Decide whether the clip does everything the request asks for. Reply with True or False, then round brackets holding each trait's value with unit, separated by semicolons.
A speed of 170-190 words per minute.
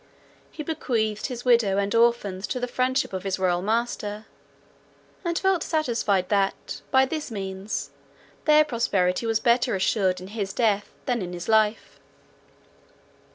False (145 wpm)